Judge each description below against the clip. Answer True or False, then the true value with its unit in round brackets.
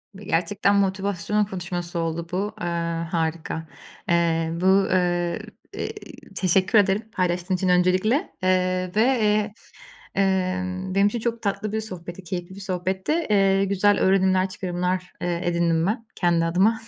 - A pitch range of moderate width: False (2.1 semitones)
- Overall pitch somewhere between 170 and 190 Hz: True (185 Hz)